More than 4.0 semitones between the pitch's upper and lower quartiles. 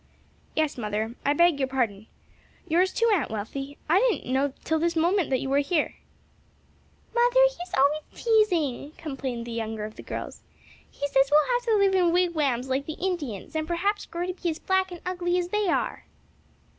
Yes: average, 5.3 semitones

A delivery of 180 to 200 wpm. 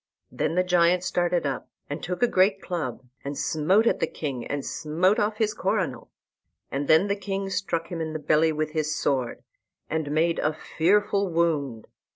Yes: average, 185 wpm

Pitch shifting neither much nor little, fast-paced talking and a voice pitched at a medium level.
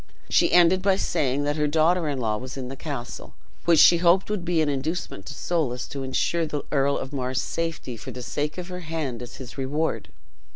Yes: average, 4.4 semitones; fast, 215 wpm; medium, 150 Hz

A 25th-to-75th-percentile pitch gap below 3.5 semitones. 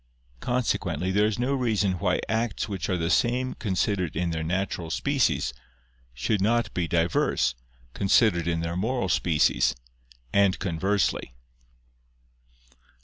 No: average, 4.8 semitones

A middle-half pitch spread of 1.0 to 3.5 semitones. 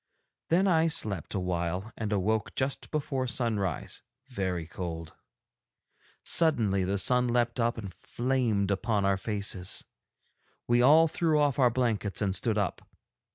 No: average, 4.8 semitones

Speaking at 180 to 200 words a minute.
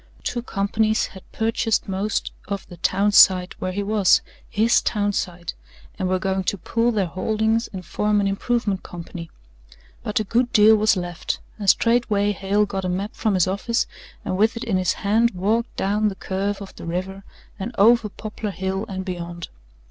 Yes: average, 185 wpm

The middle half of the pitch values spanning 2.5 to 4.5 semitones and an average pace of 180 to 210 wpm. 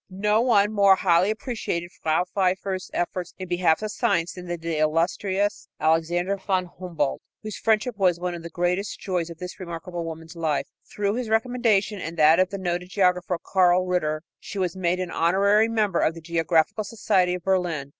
Yes: average, 2.8 semitones; average, 185 wpm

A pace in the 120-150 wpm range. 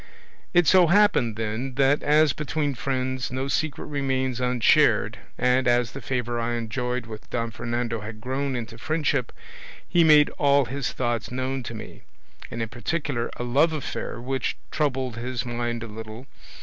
No: average, 160 wpm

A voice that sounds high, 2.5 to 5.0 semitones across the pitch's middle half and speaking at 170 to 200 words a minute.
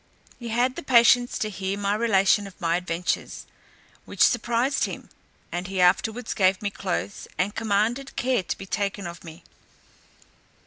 No: high, 200 Hz; average, 4.0 semitones; average, 160 wpm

